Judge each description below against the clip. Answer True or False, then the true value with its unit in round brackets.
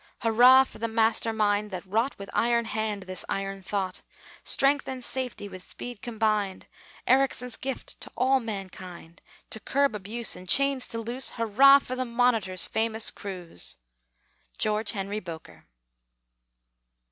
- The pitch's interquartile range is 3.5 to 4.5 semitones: True (4.0 semitones)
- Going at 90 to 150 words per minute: True (140 wpm)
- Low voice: False (220 Hz)